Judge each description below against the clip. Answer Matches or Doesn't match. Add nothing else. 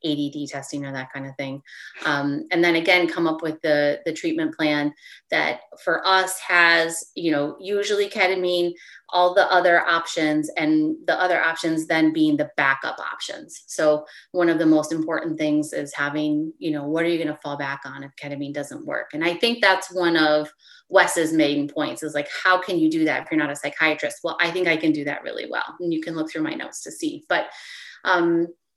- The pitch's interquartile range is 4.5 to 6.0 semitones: Doesn't match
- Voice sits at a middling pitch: Matches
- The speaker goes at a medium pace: Doesn't match